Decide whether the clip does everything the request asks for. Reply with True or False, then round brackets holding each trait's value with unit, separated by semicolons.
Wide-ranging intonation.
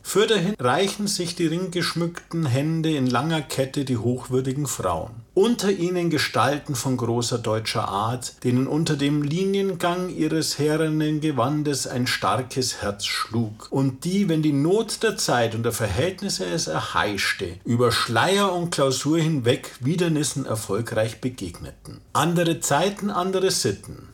True (5.8 semitones)